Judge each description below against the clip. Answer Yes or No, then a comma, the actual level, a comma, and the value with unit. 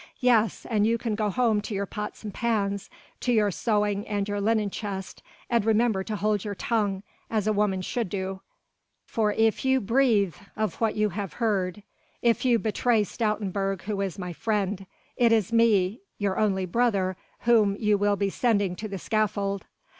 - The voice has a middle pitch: No, high, 210 Hz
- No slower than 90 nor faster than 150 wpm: No, average, 180 wpm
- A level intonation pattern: Yes, narrow, 2.2 semitones